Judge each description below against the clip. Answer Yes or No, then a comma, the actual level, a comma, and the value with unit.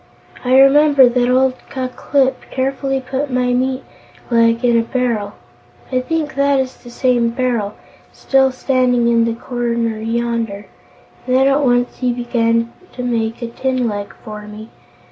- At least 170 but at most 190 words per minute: No, average, 160 wpm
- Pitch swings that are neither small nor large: No, narrow, 2.2 semitones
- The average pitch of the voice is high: Yes, high, 245 Hz